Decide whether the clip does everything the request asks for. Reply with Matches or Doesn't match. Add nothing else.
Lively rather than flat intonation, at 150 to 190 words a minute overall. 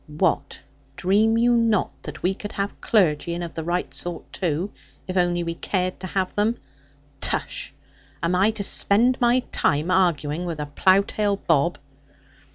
Doesn't match